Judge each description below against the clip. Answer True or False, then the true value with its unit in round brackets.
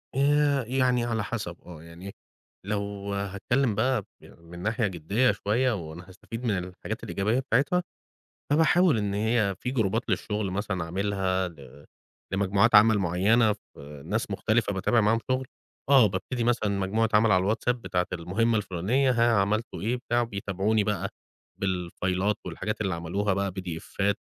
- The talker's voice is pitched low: True (105 Hz)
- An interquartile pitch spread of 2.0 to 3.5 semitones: False (3.9 semitones)